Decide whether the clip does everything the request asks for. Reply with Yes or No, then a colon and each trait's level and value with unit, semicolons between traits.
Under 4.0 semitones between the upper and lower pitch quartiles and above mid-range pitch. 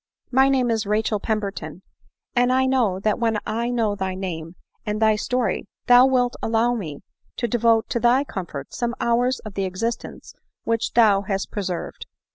Yes: average, 3.6 semitones; high, 225 Hz